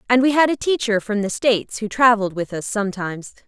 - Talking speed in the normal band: No, fast, 225 wpm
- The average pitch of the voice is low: No, high, 220 Hz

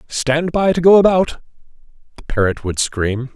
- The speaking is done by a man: Yes, male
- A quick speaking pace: No, average, 160 wpm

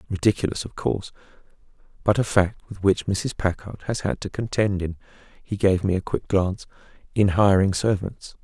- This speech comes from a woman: No, male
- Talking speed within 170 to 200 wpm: No, average, 155 wpm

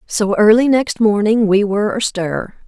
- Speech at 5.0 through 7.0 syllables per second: No, 4.5 syllables/s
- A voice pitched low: No, high, 215 Hz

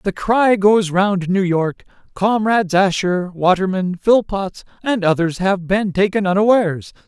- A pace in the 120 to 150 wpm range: Yes, slow, 135 wpm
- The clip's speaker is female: No, male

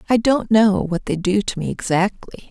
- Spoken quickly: Yes, fast, 215 wpm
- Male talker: No, female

